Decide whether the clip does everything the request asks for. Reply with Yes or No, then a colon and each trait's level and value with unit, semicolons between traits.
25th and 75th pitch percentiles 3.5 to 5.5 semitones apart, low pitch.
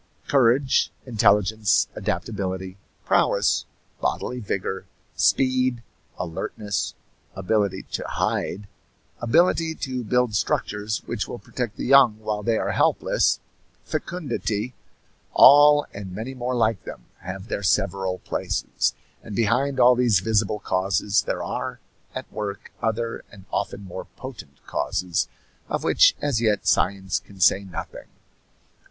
Yes: average, 4.1 semitones; low, 110 Hz